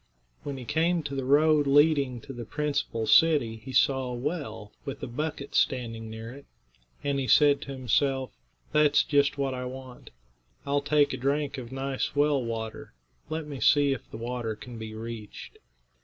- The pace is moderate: Yes, average, 180 wpm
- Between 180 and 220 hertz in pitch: No, low, 135 Hz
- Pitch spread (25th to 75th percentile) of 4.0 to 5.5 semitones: No, average, 3.2 semitones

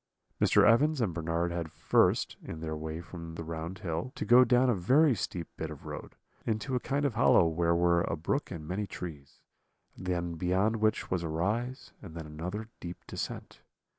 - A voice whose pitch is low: Yes, very low, 90 Hz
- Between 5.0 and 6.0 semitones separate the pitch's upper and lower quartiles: Yes, wide, 5.4 semitones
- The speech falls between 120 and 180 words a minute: No, average, 195 wpm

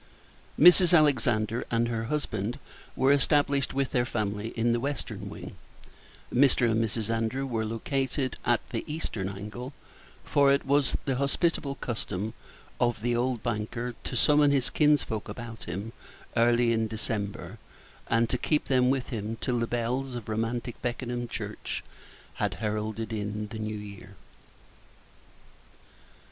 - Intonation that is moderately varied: Yes, average, 3.5 semitones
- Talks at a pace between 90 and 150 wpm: Yes, average, 140 wpm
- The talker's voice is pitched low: Yes, low, 120 Hz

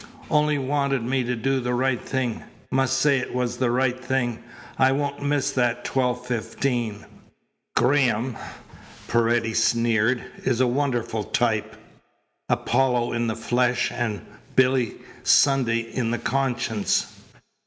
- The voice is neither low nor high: No, low, 125 Hz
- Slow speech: Yes, slow, 130 wpm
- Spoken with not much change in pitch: Yes, narrow, 2.1 semitones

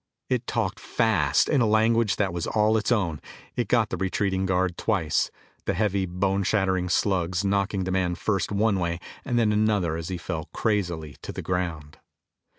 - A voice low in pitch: Yes, very low, 95 Hz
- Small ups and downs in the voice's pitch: No, average, 3.4 semitones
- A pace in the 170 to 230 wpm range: Yes, average, 180 wpm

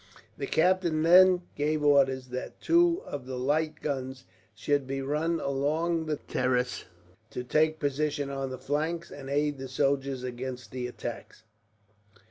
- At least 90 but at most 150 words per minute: Yes, average, 145 wpm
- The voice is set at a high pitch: No, medium, 140 Hz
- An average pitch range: Yes, average, 3.0 semitones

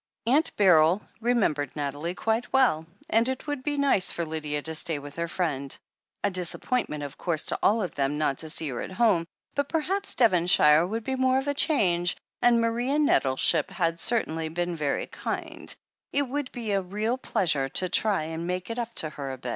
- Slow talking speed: No, average, 200 wpm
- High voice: No, medium, 180 Hz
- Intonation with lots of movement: Yes, wide, 7.4 semitones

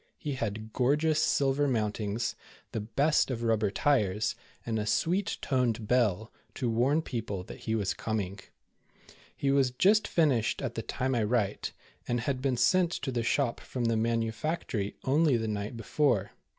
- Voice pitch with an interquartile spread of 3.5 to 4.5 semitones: Yes, average, 4.1 semitones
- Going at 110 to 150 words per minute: No, average, 165 wpm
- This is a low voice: Yes, low, 120 Hz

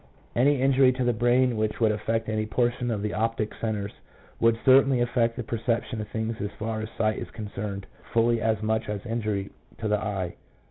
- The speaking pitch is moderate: No, low, 110 Hz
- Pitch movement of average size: No, narrow, 1.9 semitones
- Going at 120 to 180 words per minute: No, average, 200 wpm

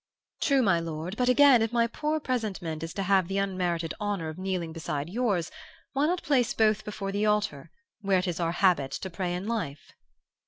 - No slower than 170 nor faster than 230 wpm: Yes, average, 200 wpm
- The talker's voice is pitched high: Yes, high, 195 Hz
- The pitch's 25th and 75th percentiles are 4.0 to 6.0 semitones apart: Yes, average, 4.8 semitones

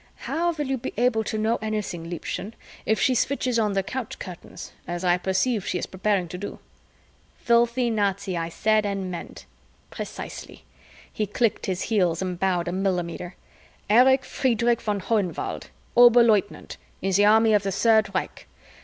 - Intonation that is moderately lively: Yes, average, 3.9 semitones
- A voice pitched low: No, high, 210 Hz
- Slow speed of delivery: No, average, 160 wpm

